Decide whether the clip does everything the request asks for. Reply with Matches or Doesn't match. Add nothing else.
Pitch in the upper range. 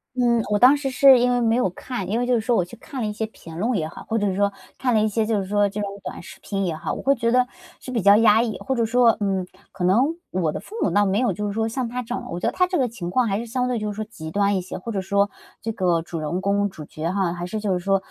Matches